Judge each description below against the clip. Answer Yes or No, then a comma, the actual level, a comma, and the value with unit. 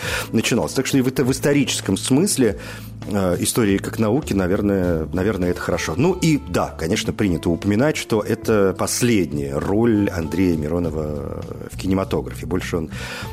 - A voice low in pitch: Yes, low, 100 Hz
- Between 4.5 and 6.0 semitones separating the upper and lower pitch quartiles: No, average, 4.1 semitones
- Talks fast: No, average, 150 wpm